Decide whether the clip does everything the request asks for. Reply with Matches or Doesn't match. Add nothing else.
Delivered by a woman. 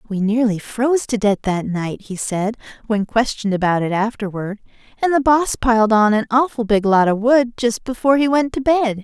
Matches